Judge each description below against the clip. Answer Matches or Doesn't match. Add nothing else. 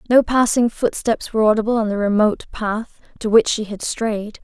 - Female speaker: Matches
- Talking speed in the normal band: Matches